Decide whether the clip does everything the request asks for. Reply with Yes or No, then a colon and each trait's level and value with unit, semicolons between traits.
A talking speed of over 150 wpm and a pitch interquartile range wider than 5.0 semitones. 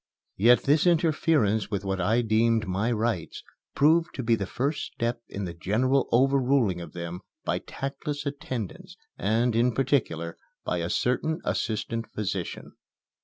No: average, 145 wpm; wide, 5.6 semitones